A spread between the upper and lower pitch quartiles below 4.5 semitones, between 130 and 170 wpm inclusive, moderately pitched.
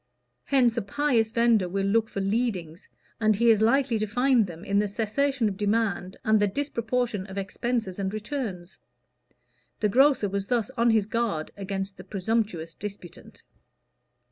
No: average, 3.3 semitones; average, 160 wpm; high, 215 Hz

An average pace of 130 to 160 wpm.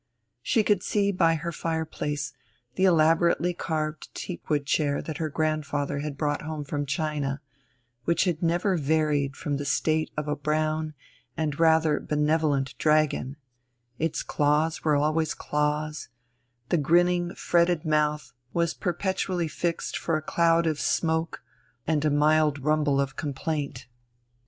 Yes: slow, 135 wpm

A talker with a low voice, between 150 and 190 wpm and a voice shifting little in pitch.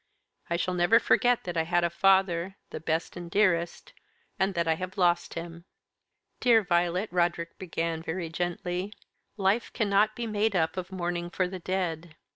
No: medium, 175 Hz; average, 170 wpm; narrow, 2.3 semitones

